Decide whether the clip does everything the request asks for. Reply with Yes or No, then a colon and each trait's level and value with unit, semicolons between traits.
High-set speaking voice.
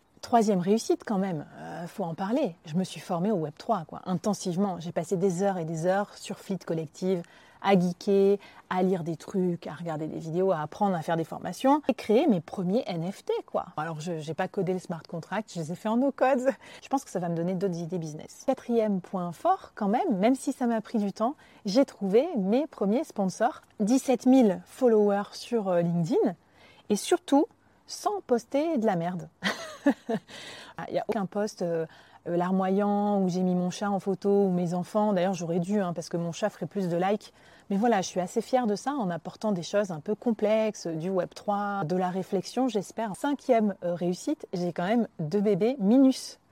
Yes: high, 195 Hz